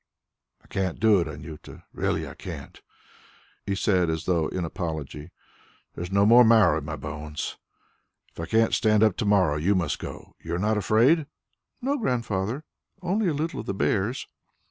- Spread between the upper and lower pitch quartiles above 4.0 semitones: Yes, average, 5.2 semitones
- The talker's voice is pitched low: Yes, low, 100 Hz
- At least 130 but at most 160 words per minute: No, average, 180 wpm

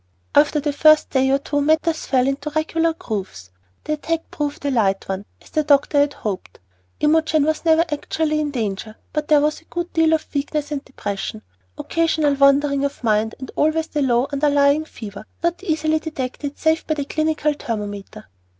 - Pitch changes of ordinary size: Yes, average, 3.0 semitones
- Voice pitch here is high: Yes, very high, 290 Hz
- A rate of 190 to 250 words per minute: No, average, 180 wpm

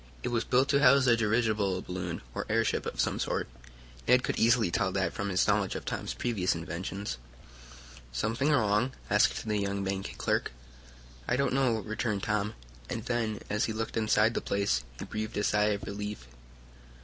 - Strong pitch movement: No, narrow, 2.6 semitones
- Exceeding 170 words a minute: Yes, average, 180 wpm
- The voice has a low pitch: Yes, low, 105 Hz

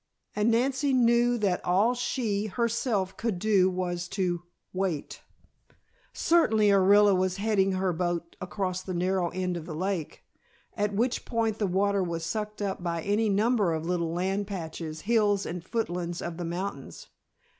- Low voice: No, high, 195 Hz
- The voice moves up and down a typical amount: Yes, average, 3.3 semitones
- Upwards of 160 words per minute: No, average, 155 wpm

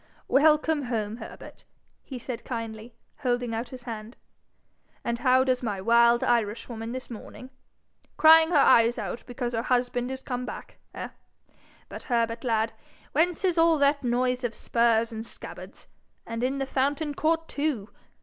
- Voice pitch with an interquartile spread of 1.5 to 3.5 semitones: Yes, average, 3.0 semitones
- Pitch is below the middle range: No, high, 245 Hz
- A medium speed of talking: Yes, average, 155 wpm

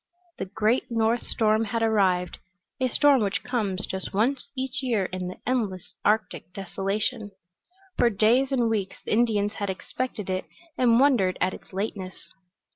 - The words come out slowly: No, average, 155 wpm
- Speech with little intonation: No, average, 3.9 semitones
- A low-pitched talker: No, high, 215 Hz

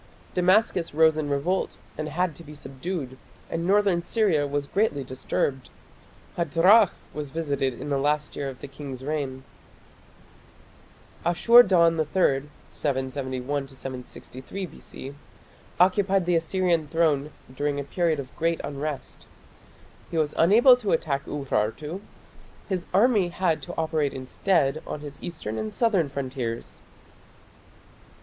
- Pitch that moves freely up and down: No, average, 4.3 semitones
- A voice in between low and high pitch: Yes, medium, 155 Hz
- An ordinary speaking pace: No, slow, 130 wpm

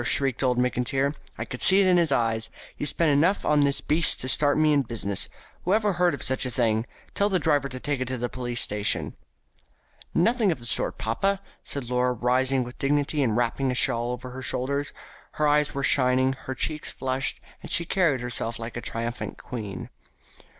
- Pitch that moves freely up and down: No, average, 3.5 semitones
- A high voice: No, low, 130 Hz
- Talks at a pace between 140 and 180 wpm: No, fast, 205 wpm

